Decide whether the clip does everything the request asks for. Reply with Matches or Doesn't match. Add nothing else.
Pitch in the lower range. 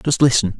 Matches